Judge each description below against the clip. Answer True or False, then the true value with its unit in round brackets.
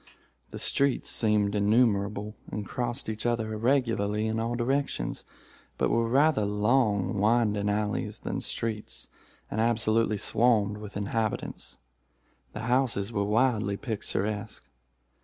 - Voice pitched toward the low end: True (110 Hz)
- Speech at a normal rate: False (120 wpm)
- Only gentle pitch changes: True (2.3 semitones)